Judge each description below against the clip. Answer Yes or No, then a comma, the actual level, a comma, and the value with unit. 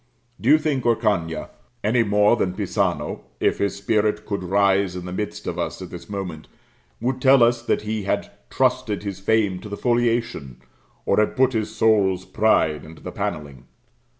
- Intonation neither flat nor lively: Yes, average, 3.8 semitones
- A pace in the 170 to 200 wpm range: Yes, average, 180 wpm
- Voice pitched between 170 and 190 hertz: No, low, 105 Hz